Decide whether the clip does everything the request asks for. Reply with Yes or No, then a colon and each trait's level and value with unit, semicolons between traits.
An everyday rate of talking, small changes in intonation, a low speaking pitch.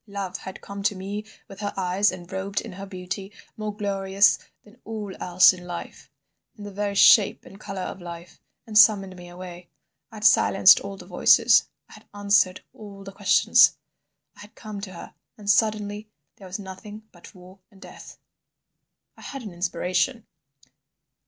No: average, 170 wpm; narrow, 2.0 semitones; high, 195 Hz